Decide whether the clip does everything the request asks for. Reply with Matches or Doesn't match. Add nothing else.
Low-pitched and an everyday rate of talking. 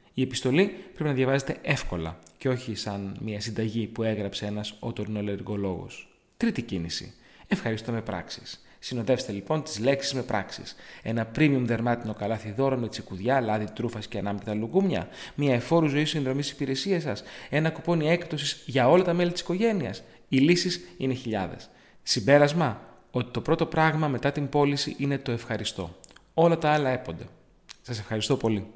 Matches